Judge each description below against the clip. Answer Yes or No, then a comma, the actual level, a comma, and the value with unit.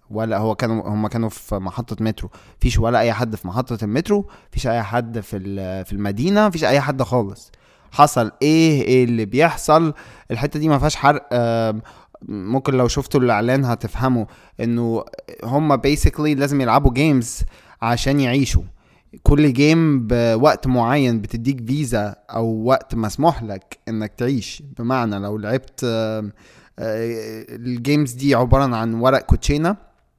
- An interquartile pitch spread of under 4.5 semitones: Yes, average, 4.0 semitones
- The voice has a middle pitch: No, low, 120 Hz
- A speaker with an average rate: No, fast, 140 wpm